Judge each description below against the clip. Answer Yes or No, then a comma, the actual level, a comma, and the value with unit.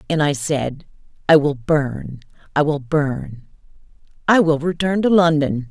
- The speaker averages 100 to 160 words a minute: Yes, average, 145 wpm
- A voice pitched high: No, medium, 150 Hz